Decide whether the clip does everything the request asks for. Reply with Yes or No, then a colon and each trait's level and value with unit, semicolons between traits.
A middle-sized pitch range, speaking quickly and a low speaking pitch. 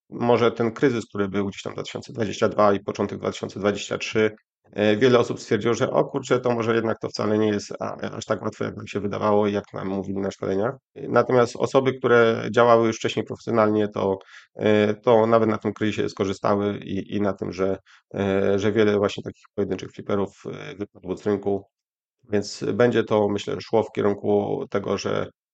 No: narrow, 2.3 semitones; fast, 170 wpm; low, 105 Hz